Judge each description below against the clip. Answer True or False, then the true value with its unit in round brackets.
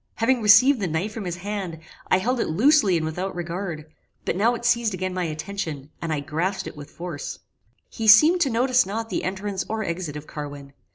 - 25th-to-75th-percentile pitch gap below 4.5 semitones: False (5.5 semitones)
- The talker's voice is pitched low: False (190 Hz)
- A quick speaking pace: True (210 wpm)